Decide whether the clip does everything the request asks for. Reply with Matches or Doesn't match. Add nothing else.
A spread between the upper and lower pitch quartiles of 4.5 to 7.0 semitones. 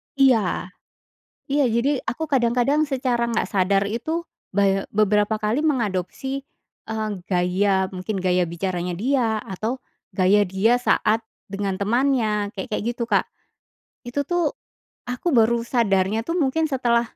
Matches